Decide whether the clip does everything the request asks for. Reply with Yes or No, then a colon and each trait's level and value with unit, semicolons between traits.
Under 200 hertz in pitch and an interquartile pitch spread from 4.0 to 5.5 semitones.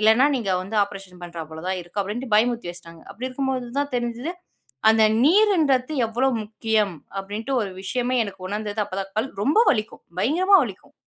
No: high, 220 Hz; average, 4.7 semitones